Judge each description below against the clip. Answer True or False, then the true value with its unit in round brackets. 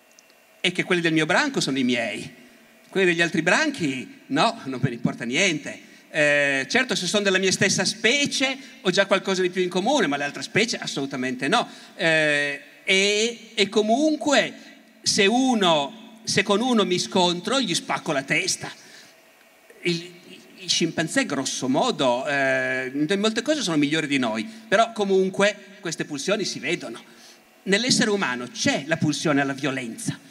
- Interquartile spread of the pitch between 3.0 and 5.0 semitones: False (5.5 semitones)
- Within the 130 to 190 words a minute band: True (160 wpm)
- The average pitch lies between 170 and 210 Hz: True (190 Hz)